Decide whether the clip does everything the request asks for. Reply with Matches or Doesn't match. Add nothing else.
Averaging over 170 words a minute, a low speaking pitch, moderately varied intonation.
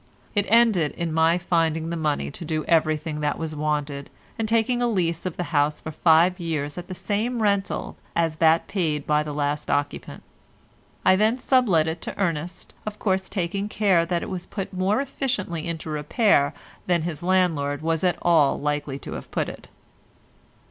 Doesn't match